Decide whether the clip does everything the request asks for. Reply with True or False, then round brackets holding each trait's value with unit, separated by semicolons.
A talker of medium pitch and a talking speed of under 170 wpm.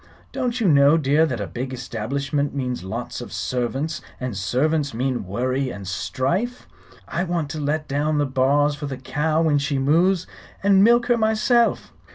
False (145 Hz; 175 wpm)